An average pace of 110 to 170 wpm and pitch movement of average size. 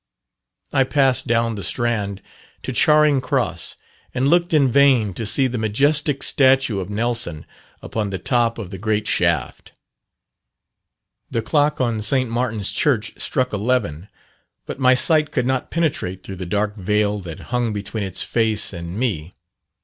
Yes: average, 155 wpm; average, 4.5 semitones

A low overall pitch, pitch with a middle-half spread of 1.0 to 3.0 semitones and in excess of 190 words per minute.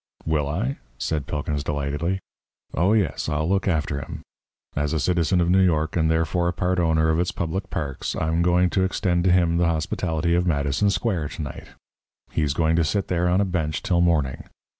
Yes: very low, 85 Hz; average, 2.7 semitones; average, 200 wpm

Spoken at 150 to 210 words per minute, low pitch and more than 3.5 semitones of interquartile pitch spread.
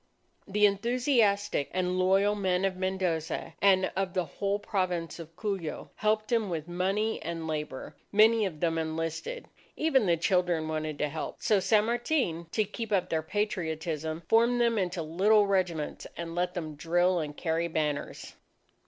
No: average, 160 wpm; medium, 185 Hz; average, 4.2 semitones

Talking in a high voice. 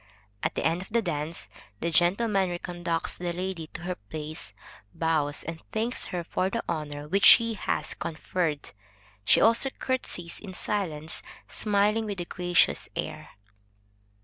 No: medium, 175 Hz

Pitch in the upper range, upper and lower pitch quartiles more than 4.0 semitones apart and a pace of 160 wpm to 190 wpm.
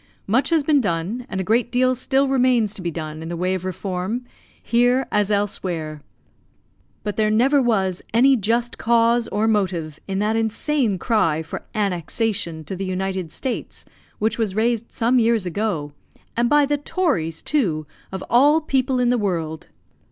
Yes: high, 215 Hz; average, 5.0 semitones; average, 170 wpm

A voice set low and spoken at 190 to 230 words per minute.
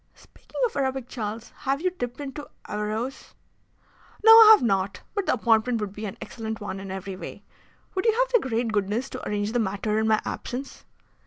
No: high, 230 Hz; average, 195 wpm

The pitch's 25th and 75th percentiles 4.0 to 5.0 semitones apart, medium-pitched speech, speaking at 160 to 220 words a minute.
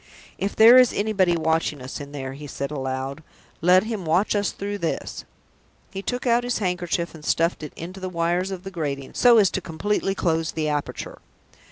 Yes: average, 4.7 semitones; medium, 175 Hz; average, 195 wpm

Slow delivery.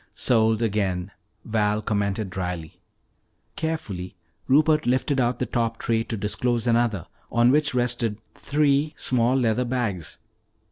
Yes: slow, 125 wpm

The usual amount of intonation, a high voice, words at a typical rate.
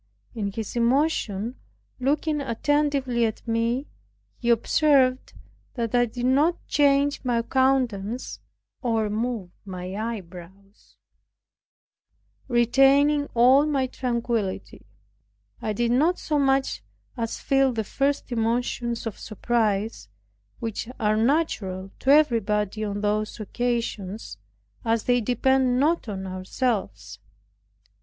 No: average, 4.0 semitones; high, 235 Hz; slow, 105 wpm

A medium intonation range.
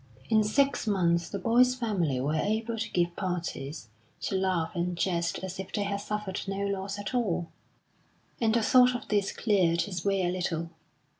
Yes: average, 3.7 semitones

